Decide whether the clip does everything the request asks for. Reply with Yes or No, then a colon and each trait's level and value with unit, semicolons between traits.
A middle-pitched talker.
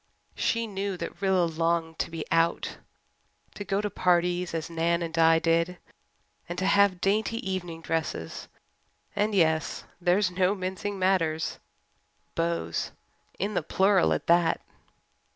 Yes: medium, 175 Hz